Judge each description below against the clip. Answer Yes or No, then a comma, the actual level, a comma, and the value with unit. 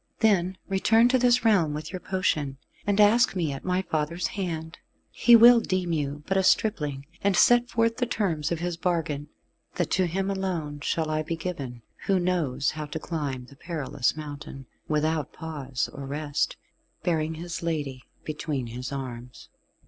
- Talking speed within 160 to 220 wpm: Yes, average, 170 wpm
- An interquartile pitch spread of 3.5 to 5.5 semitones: Yes, average, 4.6 semitones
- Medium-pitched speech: Yes, medium, 160 Hz